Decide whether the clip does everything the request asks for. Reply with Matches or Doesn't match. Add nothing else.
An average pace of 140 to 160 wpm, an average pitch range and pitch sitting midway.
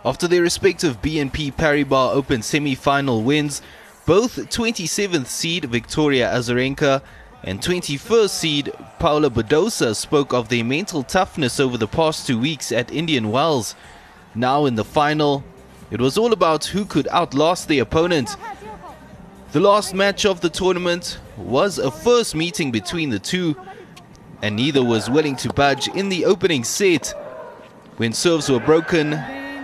Matches